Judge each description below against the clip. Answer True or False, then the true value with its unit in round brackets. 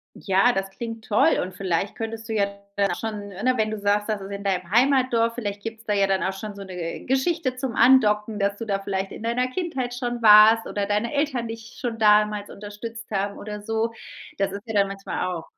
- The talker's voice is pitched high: True (210 Hz)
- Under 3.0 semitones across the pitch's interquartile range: True (2.6 semitones)